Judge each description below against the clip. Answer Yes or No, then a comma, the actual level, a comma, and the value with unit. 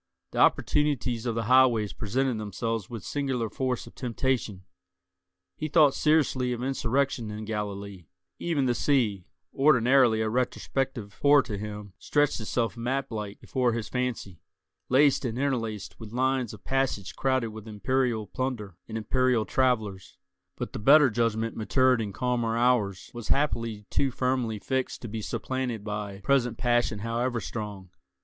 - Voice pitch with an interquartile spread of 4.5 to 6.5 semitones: No, average, 3.4 semitones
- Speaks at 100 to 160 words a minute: Yes, average, 150 wpm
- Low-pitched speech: Yes, low, 120 Hz